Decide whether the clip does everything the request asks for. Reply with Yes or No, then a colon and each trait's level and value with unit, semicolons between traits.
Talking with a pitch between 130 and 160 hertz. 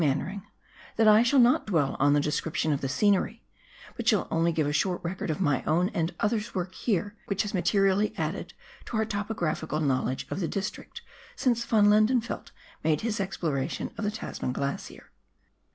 No: high, 190 Hz